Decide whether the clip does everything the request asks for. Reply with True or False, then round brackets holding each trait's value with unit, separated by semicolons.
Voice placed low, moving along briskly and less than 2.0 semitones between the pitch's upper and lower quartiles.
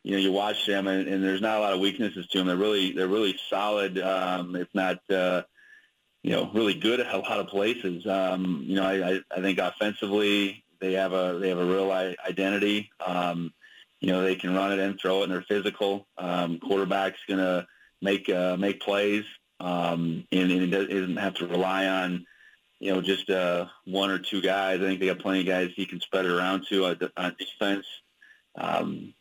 True (95 Hz; 210 wpm; 1.3 semitones)